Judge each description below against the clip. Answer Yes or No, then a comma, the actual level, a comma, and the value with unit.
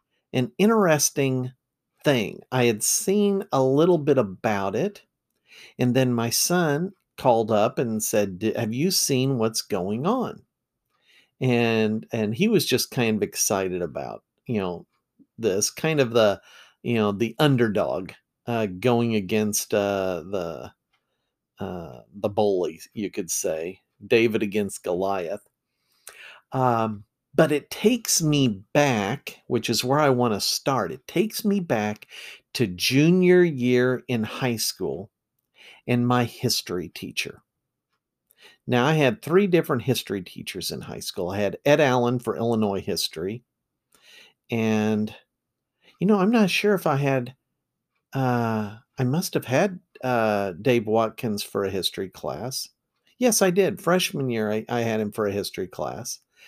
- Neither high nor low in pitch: No, low, 125 Hz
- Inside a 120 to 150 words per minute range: Yes, average, 145 wpm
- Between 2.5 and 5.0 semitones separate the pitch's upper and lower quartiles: No, wide, 5.4 semitones